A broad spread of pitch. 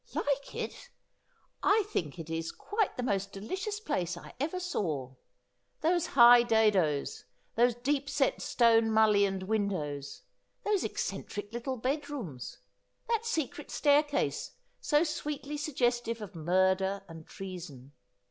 Yes: wide, 7.7 semitones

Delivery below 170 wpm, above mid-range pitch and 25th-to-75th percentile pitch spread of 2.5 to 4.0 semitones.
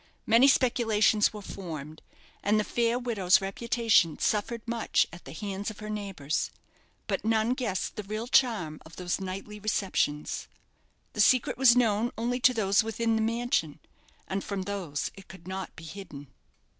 Yes: average, 160 wpm; high, 210 Hz; average, 3.7 semitones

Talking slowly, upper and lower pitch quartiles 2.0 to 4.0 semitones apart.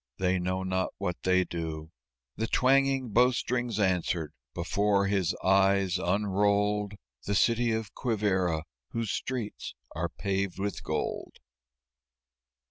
Yes: slow, 120 wpm; average, 2.9 semitones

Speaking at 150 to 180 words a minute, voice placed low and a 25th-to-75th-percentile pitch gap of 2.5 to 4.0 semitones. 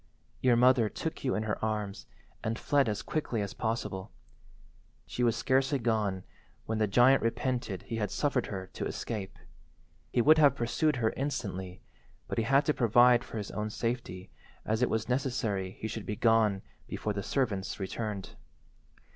Yes: average, 170 wpm; low, 115 Hz; average, 3.2 semitones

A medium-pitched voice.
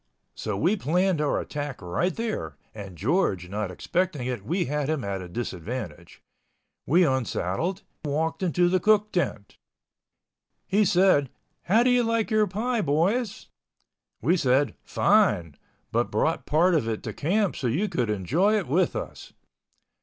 Yes: medium, 155 Hz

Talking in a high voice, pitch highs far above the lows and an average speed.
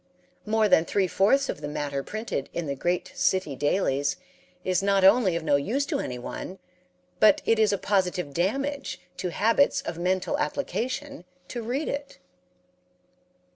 Yes: high, 195 Hz; wide, 6.5 semitones; average, 155 wpm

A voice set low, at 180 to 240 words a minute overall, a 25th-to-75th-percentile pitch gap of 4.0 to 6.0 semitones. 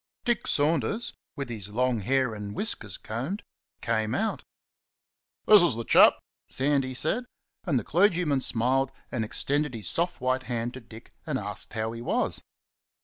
No: low, 130 Hz; average, 155 wpm; average, 4.7 semitones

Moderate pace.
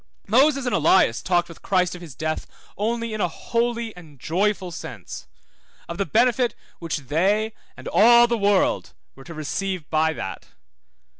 Yes: average, 160 wpm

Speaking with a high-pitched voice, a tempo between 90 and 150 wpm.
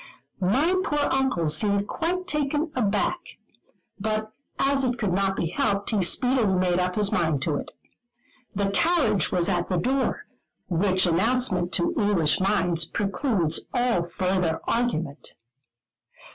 Yes: high, 200 Hz; slow, 135 wpm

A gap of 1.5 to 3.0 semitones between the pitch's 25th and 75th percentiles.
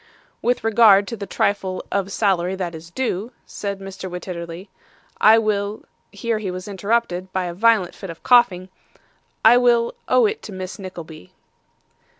No: average, 3.4 semitones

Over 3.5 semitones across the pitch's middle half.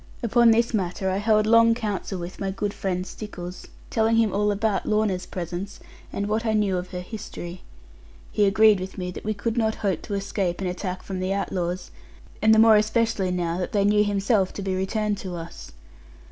No: average, 2.8 semitones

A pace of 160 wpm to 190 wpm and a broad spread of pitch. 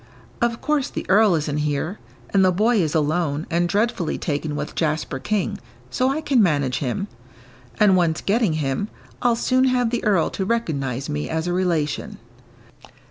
Yes: average, 170 wpm; wide, 6.8 semitones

